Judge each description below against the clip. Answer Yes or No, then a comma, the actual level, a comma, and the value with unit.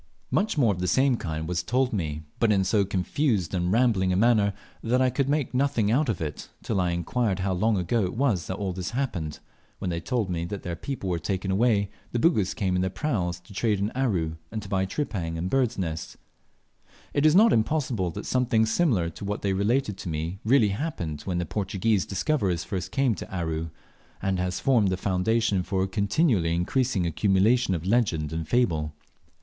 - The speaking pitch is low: Yes, low, 100 Hz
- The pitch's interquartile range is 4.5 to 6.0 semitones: Yes, average, 5.2 semitones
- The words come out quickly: Yes, fast, 210 wpm